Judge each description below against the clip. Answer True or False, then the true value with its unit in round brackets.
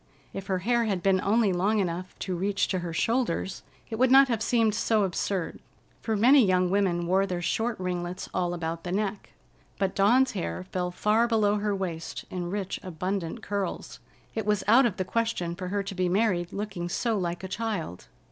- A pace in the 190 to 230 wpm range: True (195 wpm)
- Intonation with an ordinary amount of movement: True (3.3 semitones)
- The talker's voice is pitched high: True (195 Hz)